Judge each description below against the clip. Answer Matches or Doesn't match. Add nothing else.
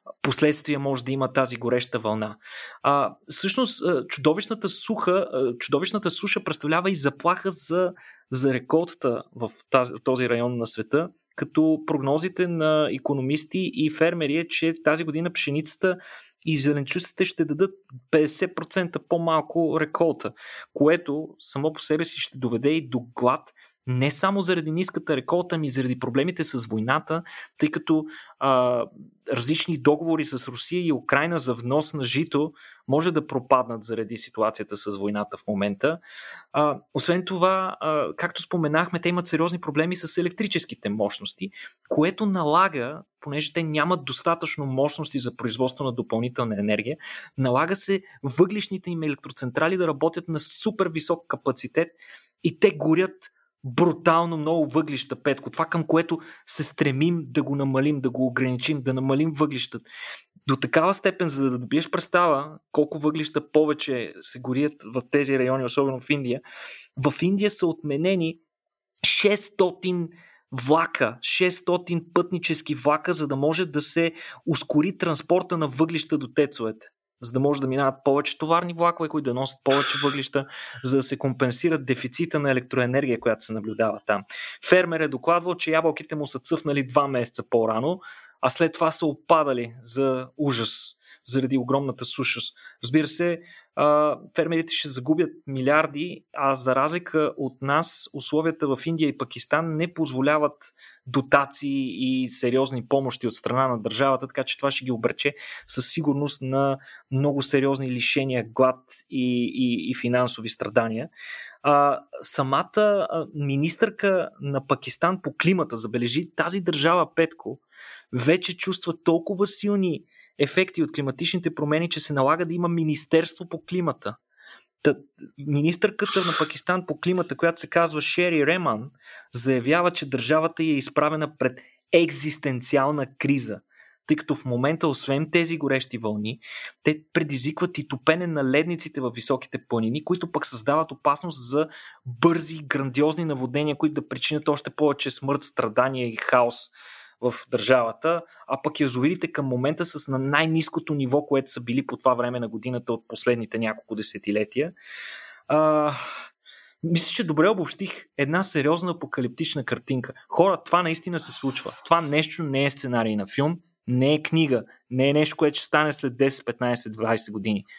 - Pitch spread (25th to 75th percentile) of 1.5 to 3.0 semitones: Doesn't match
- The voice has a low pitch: Doesn't match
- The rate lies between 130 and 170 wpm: Matches